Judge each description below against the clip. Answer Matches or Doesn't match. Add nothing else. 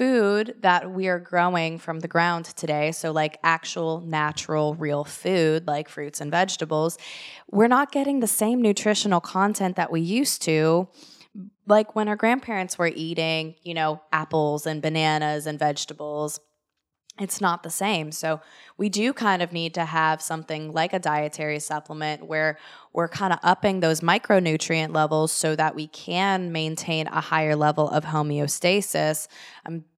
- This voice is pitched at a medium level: Matches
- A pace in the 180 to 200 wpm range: Doesn't match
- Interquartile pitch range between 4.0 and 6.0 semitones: Doesn't match